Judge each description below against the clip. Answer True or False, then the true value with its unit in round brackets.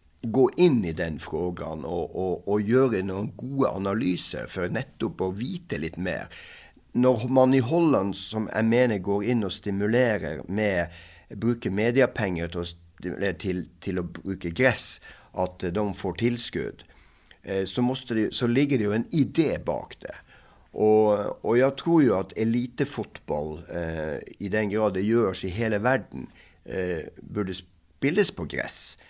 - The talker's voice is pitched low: True (105 Hz)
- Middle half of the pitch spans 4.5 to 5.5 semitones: True (4.9 semitones)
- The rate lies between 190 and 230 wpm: False (140 wpm)